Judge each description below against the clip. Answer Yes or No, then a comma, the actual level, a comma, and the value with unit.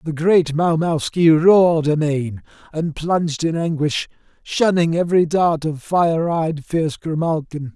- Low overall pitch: No, medium, 160 Hz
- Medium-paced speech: No, slow, 130 wpm